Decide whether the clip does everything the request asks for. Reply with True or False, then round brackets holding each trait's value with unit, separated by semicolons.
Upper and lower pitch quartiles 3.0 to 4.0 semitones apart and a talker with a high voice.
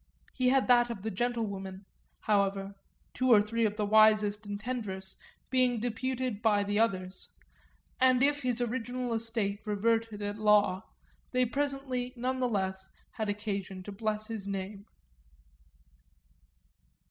True (3.3 semitones; 220 Hz)